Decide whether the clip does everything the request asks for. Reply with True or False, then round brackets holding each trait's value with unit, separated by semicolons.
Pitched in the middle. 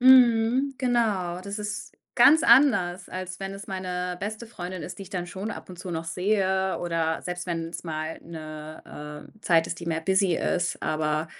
True (180 Hz)